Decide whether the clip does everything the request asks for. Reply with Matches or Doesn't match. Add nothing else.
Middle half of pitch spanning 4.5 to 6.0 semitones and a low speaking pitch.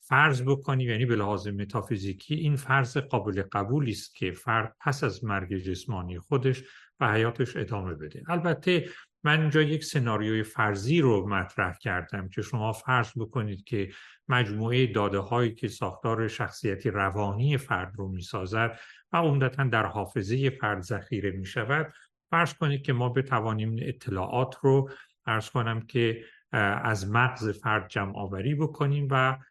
Matches